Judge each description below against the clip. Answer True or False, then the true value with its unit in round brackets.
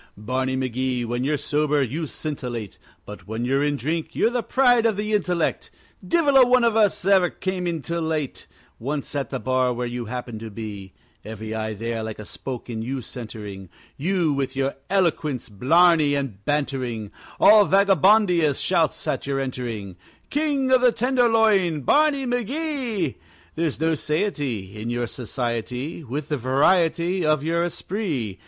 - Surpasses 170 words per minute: False (160 wpm)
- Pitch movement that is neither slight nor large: False (7.6 semitones)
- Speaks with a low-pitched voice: False (145 Hz)